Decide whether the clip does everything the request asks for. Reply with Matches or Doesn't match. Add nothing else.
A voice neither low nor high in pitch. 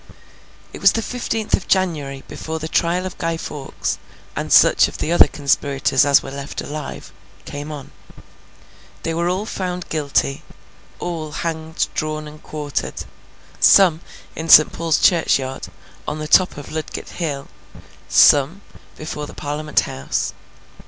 Matches